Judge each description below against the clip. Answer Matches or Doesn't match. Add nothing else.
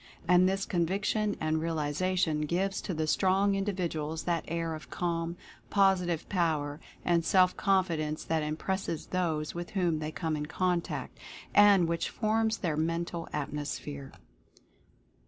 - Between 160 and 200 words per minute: Doesn't match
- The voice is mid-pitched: Matches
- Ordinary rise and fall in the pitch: Matches